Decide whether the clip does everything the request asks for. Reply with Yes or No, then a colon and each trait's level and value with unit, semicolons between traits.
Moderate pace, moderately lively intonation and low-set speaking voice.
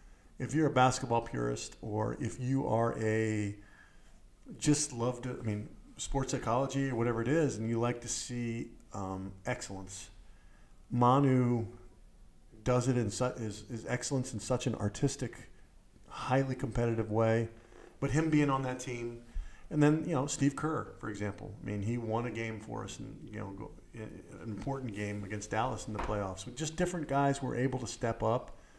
Yes: average, 175 wpm; average, 3.6 semitones; low, 115 Hz